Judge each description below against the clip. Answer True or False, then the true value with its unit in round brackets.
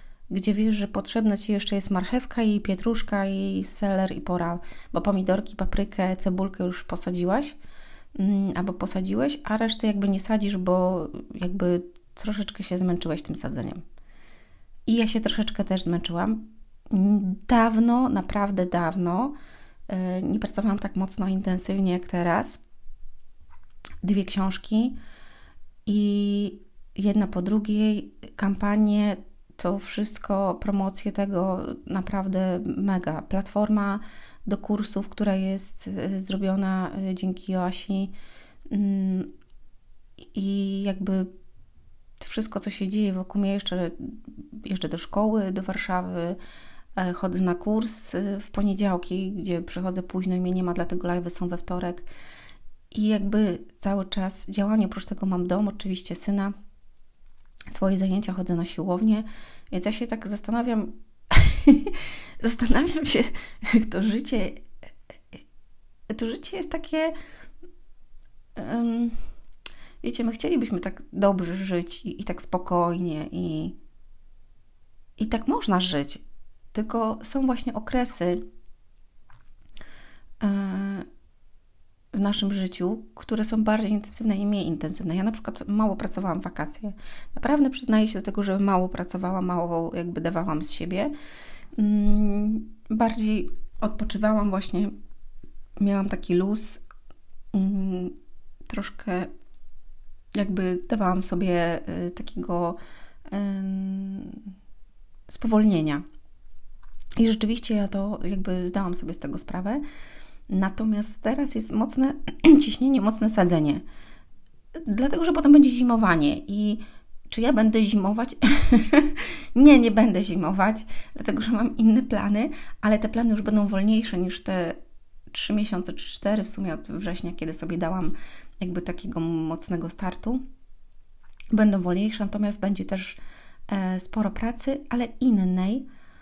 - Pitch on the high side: True (200 Hz)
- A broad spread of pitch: False (3.1 semitones)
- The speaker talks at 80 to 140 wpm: True (115 wpm)